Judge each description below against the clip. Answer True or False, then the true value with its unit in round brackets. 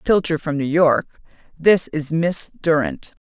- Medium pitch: True (160 Hz)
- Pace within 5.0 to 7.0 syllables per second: False (3.9 syllables/s)